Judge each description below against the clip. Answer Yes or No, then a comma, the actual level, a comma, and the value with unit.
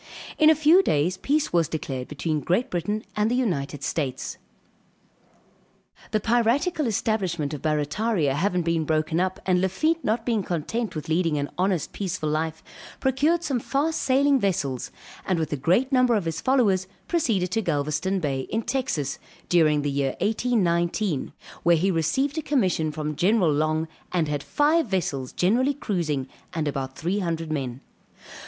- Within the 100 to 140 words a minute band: No, average, 160 wpm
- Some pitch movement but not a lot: No, wide, 7.2 semitones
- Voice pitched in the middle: Yes, medium, 180 Hz